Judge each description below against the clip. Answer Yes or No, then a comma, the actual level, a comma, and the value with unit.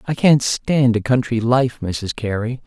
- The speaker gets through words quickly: No, average, 180 wpm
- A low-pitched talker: Yes, low, 120 Hz